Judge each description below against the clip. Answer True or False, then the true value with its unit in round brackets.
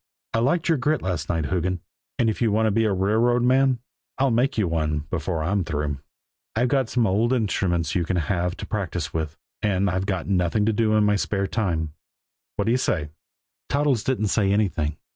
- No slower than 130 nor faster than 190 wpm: False (200 wpm)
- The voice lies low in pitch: True (100 Hz)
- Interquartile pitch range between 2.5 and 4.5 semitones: False (5.0 semitones)